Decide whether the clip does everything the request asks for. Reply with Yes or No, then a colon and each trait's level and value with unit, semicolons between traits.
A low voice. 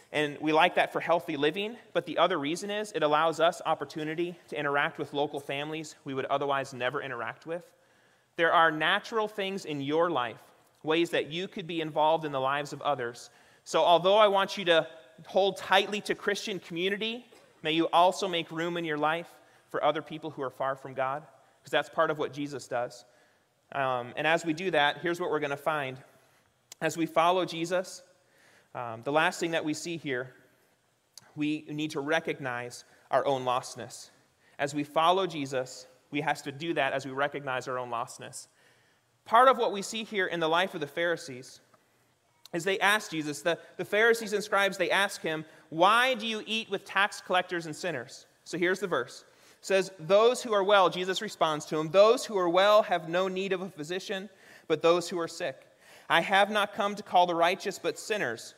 No: medium, 165 Hz